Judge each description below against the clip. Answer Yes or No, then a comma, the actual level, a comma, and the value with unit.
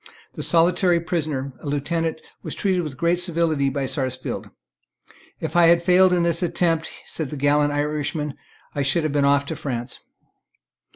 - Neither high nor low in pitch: Yes, medium, 155 Hz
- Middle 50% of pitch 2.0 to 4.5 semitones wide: Yes, average, 3.2 semitones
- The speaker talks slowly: No, average, 165 wpm